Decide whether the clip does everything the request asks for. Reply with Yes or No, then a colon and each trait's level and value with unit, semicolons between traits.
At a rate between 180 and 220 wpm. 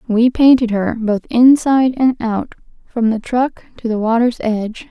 No: average, 170 wpm